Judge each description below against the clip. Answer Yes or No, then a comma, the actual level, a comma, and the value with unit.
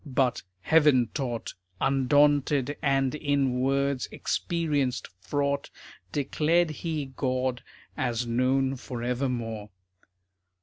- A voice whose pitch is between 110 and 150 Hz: Yes, low, 135 Hz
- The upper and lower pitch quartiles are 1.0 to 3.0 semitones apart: Yes, narrow, 2.4 semitones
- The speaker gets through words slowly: Yes, slow, 85 wpm